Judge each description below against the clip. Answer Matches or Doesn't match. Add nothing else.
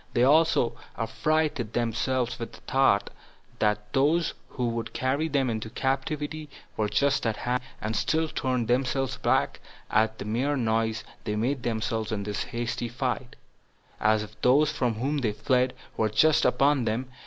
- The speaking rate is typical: Matches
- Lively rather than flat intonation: Doesn't match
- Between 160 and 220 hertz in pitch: Doesn't match